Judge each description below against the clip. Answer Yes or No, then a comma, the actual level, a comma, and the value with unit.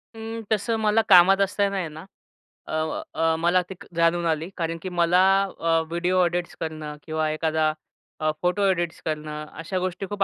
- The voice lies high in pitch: No, medium, 175 Hz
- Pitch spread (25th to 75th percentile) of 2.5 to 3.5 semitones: Yes, average, 3.0 semitones